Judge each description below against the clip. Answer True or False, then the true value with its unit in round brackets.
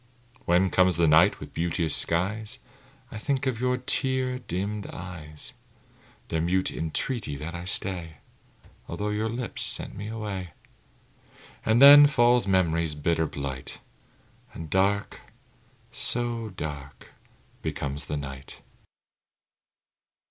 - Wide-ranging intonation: True (5.8 semitones)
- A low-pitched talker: True (95 Hz)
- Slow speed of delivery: True (115 wpm)